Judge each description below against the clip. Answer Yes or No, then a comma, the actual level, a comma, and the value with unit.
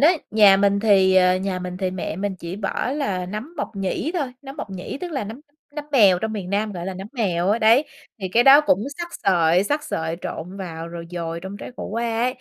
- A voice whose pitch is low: No, high, 200 Hz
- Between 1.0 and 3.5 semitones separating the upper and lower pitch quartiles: No, average, 4.3 semitones